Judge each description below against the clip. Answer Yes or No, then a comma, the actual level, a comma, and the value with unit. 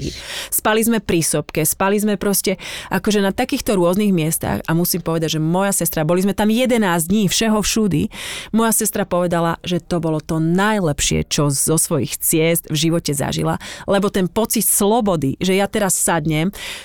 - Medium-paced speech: No, fast, 170 wpm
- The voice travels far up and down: No, average, 4.4 semitones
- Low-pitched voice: No, medium, 180 Hz